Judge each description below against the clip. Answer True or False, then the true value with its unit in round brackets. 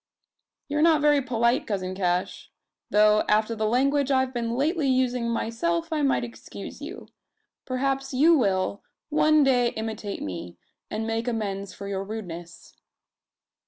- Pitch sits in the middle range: False (235 Hz)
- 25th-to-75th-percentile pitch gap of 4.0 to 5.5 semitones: True (4.7 semitones)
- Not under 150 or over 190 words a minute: False (140 wpm)